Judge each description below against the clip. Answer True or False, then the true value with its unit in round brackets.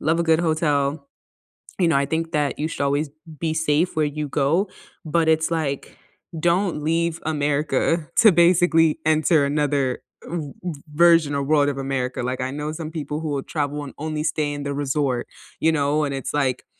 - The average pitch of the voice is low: False (150 Hz)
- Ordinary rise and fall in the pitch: False (2.3 semitones)